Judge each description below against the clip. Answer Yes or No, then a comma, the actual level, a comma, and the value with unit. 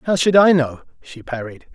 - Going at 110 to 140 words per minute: No, fast, 205 wpm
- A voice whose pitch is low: No, medium, 145 Hz